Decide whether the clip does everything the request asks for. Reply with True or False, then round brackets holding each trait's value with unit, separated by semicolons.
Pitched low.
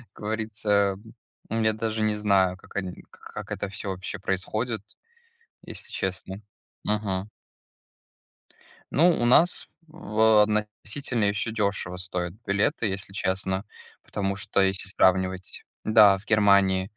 True (100 Hz)